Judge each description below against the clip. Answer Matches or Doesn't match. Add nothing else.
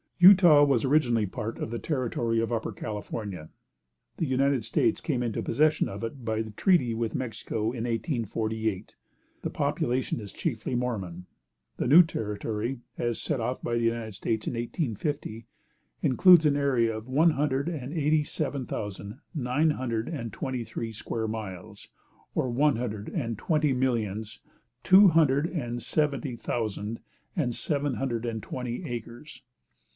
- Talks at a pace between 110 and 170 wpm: Matches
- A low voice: Matches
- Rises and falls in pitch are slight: Doesn't match